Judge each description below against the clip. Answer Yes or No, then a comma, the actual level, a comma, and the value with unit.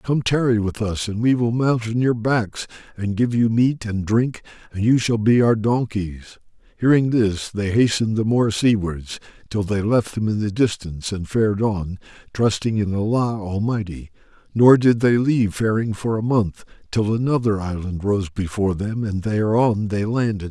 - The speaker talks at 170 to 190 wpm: Yes, average, 180 wpm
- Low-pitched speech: Yes, low, 110 Hz